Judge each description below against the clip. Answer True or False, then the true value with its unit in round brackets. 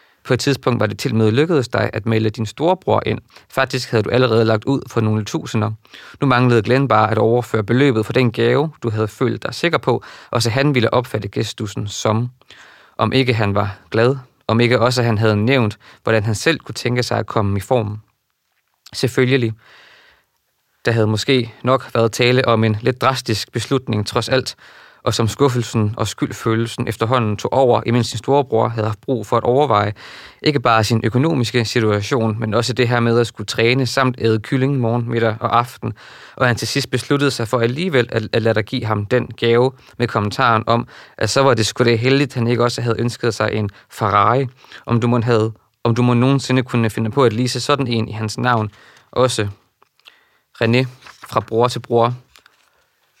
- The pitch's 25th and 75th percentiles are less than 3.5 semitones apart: True (2.5 semitones)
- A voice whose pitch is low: True (120 Hz)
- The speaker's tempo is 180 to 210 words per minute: True (200 wpm)